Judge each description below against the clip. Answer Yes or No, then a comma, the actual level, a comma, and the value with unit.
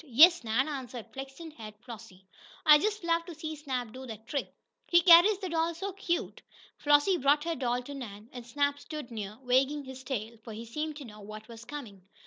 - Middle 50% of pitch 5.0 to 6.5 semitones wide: Yes, average, 5.3 semitones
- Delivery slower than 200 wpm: No, fast, 205 wpm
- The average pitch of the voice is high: Yes, very high, 270 Hz